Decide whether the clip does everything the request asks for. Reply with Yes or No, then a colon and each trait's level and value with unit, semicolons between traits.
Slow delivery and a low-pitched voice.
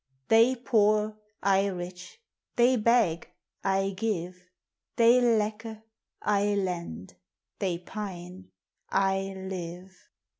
No: slow, 90 wpm; high, 195 Hz